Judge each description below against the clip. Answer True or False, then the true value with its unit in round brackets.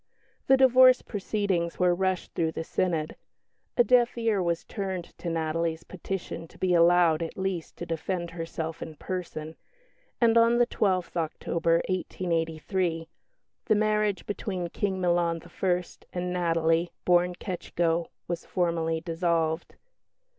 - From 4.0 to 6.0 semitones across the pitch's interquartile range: False (2.4 semitones)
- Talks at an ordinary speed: False (130 wpm)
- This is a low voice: False (175 Hz)